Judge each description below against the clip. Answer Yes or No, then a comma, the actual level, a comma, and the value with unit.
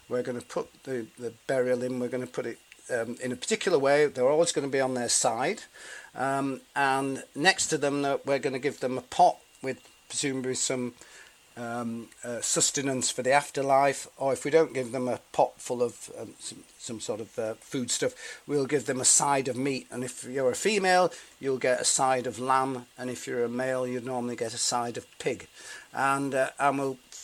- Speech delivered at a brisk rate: Yes, fast, 220 wpm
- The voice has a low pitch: Yes, low, 130 Hz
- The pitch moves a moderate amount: No, narrow, 1.9 semitones